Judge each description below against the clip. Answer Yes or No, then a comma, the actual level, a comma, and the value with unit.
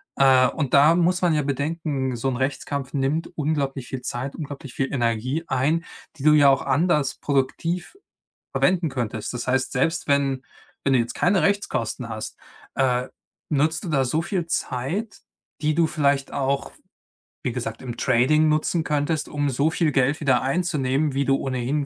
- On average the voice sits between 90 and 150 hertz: Yes, medium, 140 Hz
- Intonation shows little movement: No, average, 3.1 semitones